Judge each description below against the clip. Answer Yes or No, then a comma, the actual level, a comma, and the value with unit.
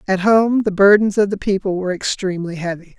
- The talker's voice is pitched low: No, high, 195 Hz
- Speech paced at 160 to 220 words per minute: Yes, average, 200 wpm